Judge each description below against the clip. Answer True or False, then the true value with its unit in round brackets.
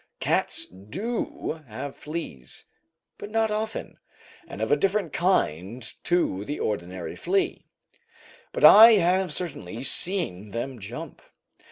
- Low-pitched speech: False (150 Hz)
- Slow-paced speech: True (120 wpm)